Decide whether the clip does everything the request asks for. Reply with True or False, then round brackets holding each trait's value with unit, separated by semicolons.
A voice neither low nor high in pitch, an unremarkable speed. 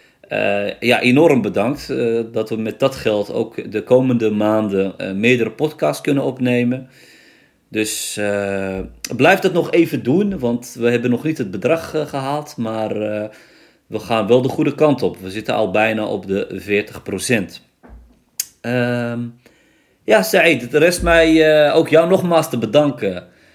False (120 Hz; 160 wpm)